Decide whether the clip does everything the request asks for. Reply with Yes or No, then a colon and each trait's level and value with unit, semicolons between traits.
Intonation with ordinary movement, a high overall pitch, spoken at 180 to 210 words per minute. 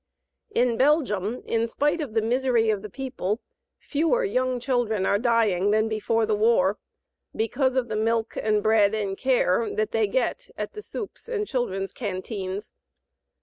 No: average, 3.5 semitones; high, 225 Hz; average, 160 wpm